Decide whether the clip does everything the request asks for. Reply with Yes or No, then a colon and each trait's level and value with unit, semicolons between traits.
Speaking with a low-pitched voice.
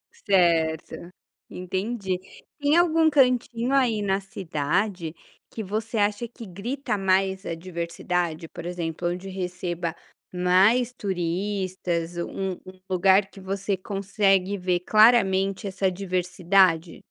No: high, 190 Hz